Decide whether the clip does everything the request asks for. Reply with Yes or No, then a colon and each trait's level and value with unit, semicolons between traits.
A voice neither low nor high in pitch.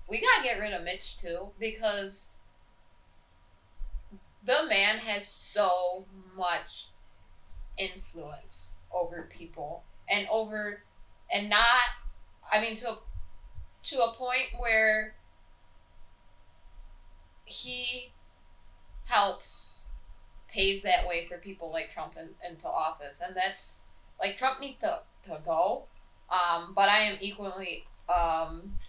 Yes: medium, 180 Hz